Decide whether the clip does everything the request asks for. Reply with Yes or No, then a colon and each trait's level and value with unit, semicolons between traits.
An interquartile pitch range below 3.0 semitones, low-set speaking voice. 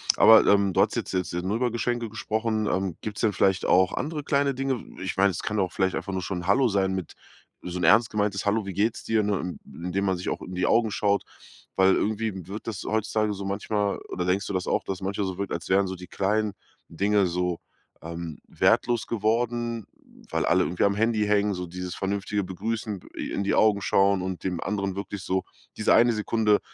Yes: narrow, 2.6 semitones; low, 100 Hz